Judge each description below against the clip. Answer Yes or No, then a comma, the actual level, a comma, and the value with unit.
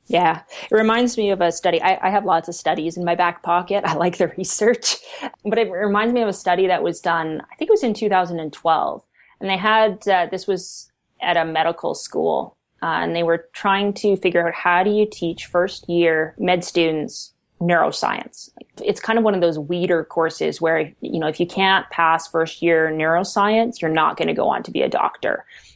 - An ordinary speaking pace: No, fast, 215 wpm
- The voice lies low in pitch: No, medium, 175 Hz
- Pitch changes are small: No, average, 3.3 semitones